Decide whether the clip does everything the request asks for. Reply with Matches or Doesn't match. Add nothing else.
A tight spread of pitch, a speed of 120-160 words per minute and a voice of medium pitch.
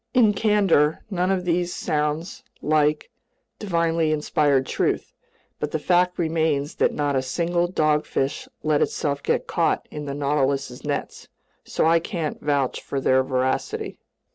Doesn't match